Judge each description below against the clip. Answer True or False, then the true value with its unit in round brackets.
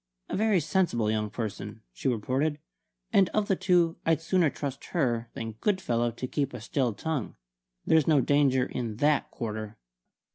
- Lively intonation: True (5.9 semitones)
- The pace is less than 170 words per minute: True (160 wpm)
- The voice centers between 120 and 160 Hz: True (135 Hz)